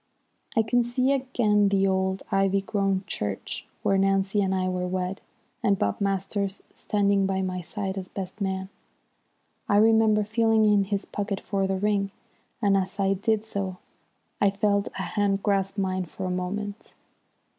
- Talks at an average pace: Yes, average, 165 wpm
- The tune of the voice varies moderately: No, narrow, 1.5 semitones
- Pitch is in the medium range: No, high, 195 Hz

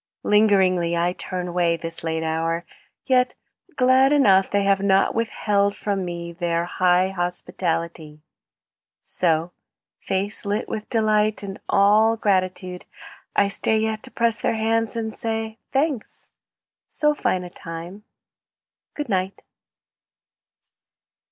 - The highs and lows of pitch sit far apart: No, average, 3.9 semitones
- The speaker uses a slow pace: Yes, slow, 125 wpm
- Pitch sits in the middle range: No, high, 195 Hz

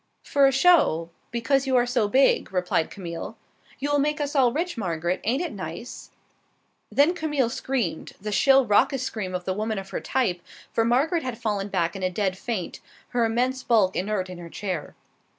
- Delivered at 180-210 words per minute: Yes, average, 190 wpm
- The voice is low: No, high, 230 Hz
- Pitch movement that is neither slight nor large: No, wide, 6.4 semitones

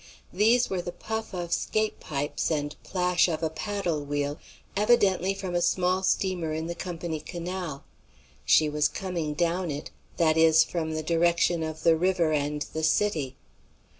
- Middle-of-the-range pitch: Yes, medium, 170 Hz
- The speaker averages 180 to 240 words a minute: No, average, 165 wpm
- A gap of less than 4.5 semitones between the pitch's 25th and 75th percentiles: Yes, average, 2.9 semitones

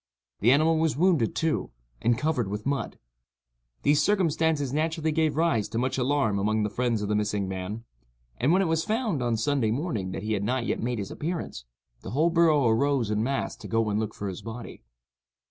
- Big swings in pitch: Yes, wide, 6.5 semitones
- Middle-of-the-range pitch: No, low, 125 Hz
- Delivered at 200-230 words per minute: Yes, fast, 205 wpm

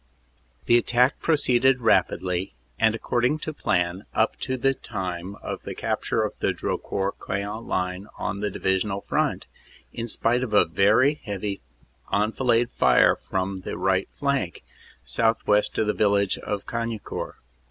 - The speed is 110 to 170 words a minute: Yes, average, 140 wpm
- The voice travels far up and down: No, average, 3.6 semitones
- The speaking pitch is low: Yes, low, 105 Hz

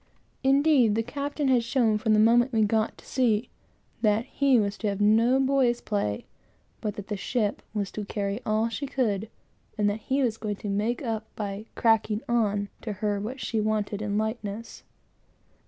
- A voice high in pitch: Yes, high, 220 Hz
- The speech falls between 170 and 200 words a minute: Yes, average, 190 wpm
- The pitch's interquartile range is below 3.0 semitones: Yes, narrow, 2.6 semitones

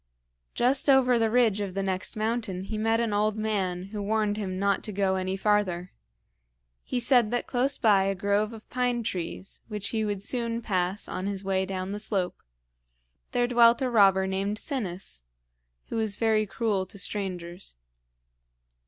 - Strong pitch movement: No, average, 3.2 semitones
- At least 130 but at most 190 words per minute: Yes, average, 170 wpm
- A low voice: No, high, 205 Hz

